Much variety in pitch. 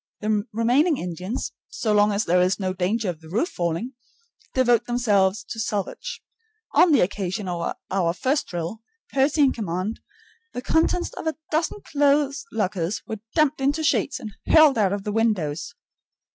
Yes: wide, 6.6 semitones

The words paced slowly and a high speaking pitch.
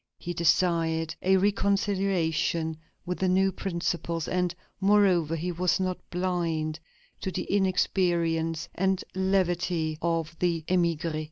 No: slow, 115 wpm; medium, 175 Hz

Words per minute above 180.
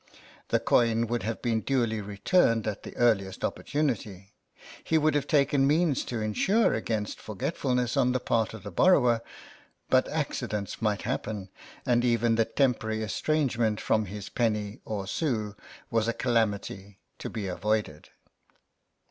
No: average, 150 wpm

